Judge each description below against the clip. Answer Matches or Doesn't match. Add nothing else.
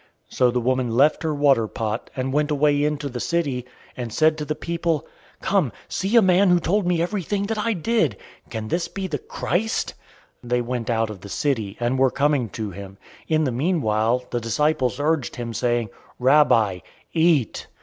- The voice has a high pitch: Doesn't match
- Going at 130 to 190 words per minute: Doesn't match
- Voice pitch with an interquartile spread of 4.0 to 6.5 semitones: Matches